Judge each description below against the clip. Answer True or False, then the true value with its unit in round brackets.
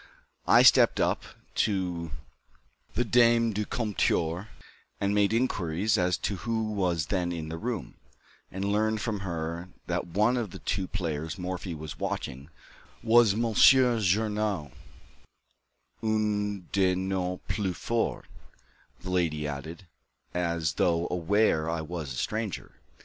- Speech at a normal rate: False (130 wpm)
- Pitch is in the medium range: False (95 Hz)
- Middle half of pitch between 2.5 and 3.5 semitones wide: False (4.2 semitones)